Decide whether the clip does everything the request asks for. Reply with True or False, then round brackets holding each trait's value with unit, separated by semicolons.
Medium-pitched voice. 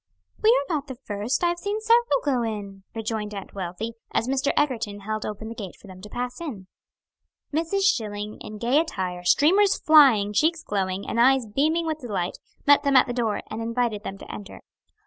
False (235 Hz)